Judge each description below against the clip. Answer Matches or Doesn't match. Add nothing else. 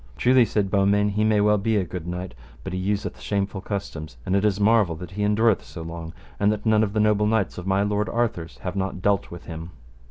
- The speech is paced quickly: Matches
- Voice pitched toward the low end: Matches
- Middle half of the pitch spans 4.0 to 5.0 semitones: Doesn't match